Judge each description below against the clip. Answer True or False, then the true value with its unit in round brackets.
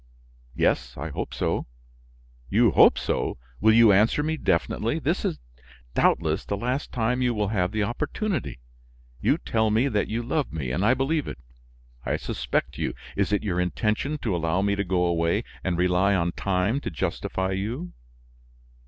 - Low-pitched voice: True (100 Hz)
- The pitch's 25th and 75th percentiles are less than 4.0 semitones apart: False (5.0 semitones)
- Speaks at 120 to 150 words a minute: False (170 wpm)